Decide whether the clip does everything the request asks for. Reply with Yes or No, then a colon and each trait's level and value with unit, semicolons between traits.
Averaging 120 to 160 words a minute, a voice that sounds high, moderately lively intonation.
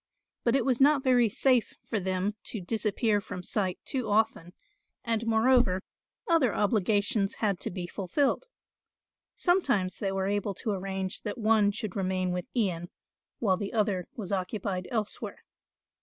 Yes: average, 150 wpm; high, 205 Hz; average, 3.5 semitones